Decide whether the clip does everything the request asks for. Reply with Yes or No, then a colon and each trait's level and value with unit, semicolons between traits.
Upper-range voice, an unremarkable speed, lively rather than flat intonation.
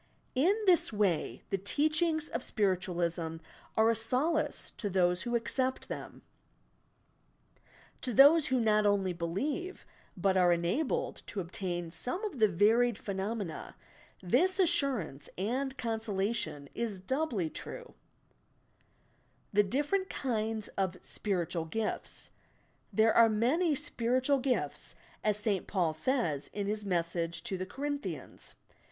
No: high, 220 Hz; slow, 120 wpm; wide, 6.3 semitones